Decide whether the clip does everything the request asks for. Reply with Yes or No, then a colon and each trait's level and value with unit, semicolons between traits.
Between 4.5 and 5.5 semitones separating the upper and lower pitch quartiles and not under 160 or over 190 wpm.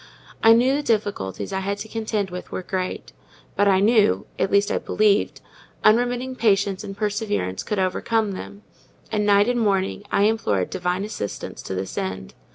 No: average, 2.7 semitones; average, 170 wpm